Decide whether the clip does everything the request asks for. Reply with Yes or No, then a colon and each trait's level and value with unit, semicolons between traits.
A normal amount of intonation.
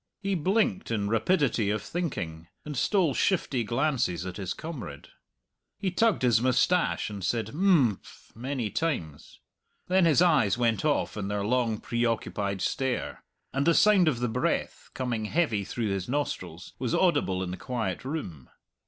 No: wide, 7.8 semitones